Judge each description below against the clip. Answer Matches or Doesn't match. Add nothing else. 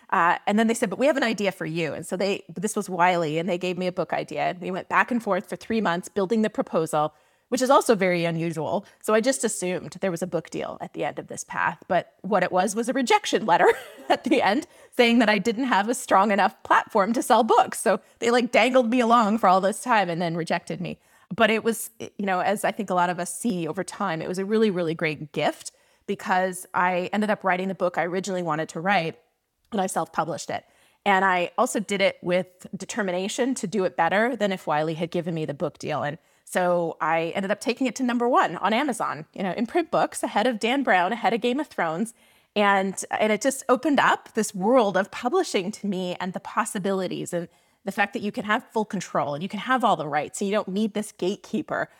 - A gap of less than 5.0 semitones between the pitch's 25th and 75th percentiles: Matches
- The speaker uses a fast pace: Matches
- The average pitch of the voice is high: Matches